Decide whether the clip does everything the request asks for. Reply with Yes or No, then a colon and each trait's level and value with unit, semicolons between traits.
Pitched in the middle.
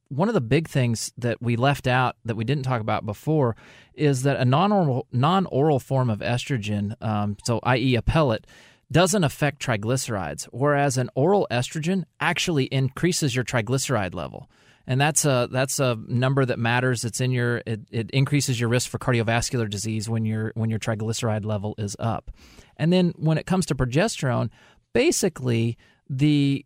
No: low, 125 Hz